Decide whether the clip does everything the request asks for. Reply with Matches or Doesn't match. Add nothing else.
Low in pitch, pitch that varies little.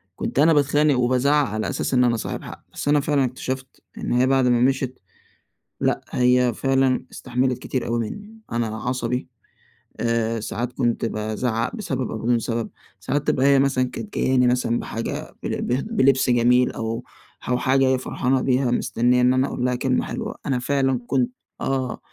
Matches